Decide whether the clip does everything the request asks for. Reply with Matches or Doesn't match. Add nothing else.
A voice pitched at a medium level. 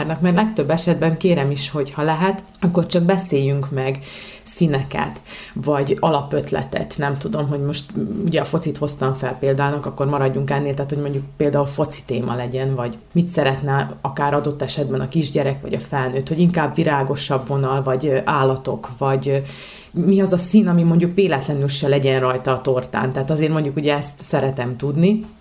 Matches